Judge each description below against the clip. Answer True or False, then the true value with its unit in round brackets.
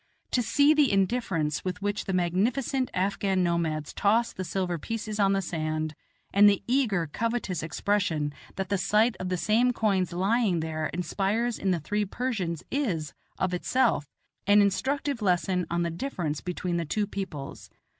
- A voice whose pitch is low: False (195 Hz)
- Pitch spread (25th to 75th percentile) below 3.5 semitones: False (4.5 semitones)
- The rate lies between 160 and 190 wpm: True (165 wpm)